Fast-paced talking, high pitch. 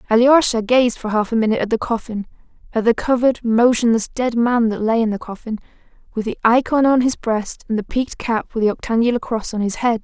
Yes: fast, 220 wpm; high, 230 Hz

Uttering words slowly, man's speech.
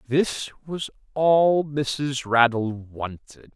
Yes: slow, 100 wpm; male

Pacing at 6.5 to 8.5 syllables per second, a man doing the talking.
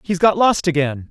No: 5.0 syllables/s; male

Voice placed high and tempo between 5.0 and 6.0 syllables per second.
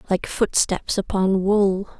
No: high, 195 Hz; 3.5 syllables/s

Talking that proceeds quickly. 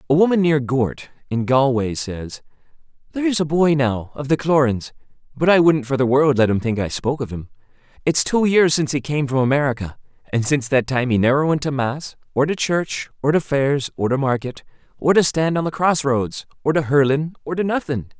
Yes: fast, 220 wpm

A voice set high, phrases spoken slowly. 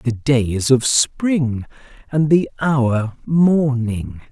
No: low, 130 Hz; slow, 125 wpm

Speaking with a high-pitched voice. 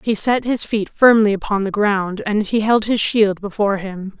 Yes: high, 210 Hz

